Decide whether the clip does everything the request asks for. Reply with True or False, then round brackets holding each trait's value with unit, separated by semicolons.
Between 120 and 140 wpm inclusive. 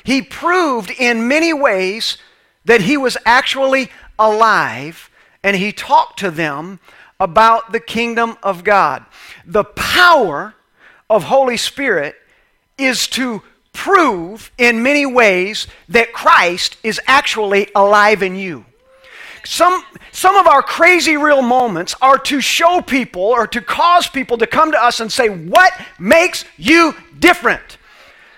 True (135 wpm)